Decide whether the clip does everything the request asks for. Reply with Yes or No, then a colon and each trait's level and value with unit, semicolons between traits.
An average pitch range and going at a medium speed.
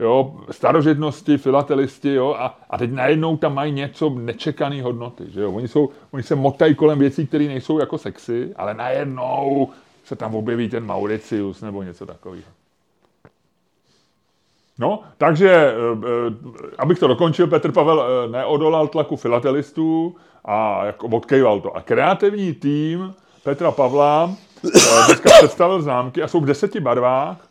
Yes: average, 4.5 semitones; average, 145 wpm